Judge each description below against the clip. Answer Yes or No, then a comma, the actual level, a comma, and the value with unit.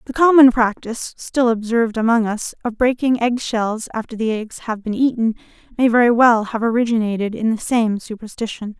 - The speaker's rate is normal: Yes, average, 175 wpm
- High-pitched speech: Yes, high, 230 Hz